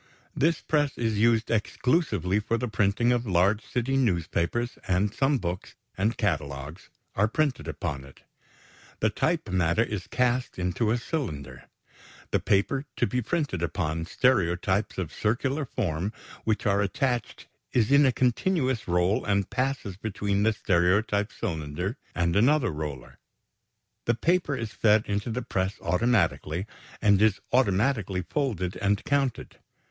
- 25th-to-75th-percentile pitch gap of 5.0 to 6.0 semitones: Yes, wide, 5.5 semitones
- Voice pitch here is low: Yes, low, 105 Hz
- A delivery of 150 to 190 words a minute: No, average, 140 wpm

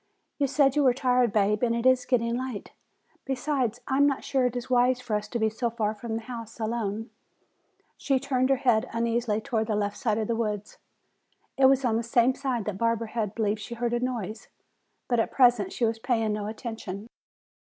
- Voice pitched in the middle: No, high, 235 Hz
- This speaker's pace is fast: Yes, fast, 215 wpm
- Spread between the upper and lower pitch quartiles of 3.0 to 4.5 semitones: No, narrow, 2.6 semitones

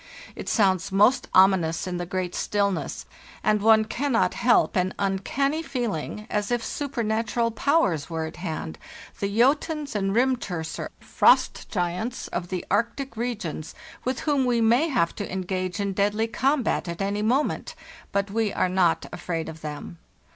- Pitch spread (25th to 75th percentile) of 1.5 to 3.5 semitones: No, average, 4.7 semitones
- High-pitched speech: Yes, high, 205 Hz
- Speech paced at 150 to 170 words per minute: Yes, average, 155 wpm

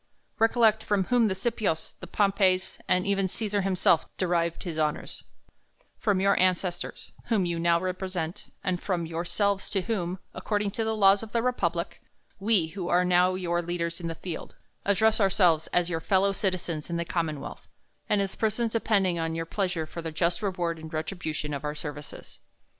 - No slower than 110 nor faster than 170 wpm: No, average, 180 wpm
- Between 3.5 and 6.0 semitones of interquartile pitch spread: No, average, 2.9 semitones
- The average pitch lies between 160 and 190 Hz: Yes, medium, 185 Hz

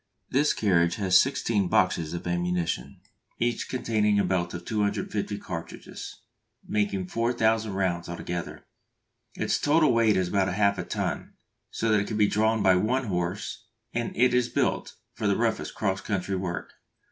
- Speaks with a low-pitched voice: Yes, low, 100 Hz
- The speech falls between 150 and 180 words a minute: Yes, average, 160 wpm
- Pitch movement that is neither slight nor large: Yes, average, 3.8 semitones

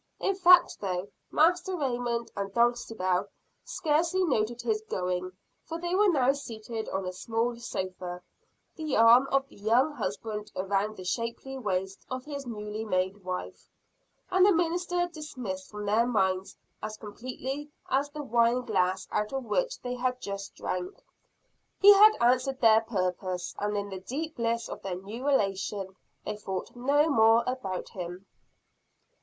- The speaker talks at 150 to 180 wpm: Yes, average, 155 wpm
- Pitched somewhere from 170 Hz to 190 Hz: No, high, 230 Hz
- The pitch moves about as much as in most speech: No, wide, 6.0 semitones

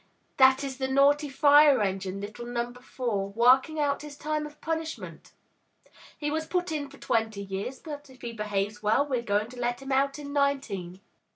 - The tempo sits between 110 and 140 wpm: No, average, 185 wpm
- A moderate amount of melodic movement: Yes, average, 4.7 semitones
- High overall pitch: Yes, very high, 265 Hz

